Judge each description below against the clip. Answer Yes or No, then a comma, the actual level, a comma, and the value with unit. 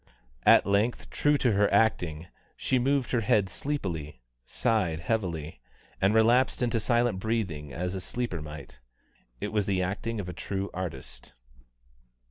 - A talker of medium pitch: No, low, 100 Hz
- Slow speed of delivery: No, average, 145 wpm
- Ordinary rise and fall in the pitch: Yes, average, 4.8 semitones